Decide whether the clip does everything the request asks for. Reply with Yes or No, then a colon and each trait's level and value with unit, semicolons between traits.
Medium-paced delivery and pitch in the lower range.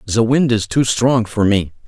No: fast, 225 wpm; low, 115 Hz